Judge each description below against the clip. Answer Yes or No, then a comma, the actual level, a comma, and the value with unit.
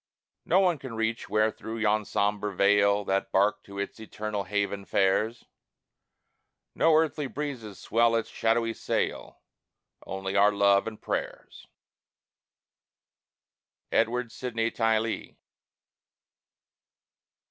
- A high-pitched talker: No, low, 110 Hz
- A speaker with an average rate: No, slow, 105 wpm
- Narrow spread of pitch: Yes, narrow, 2.3 semitones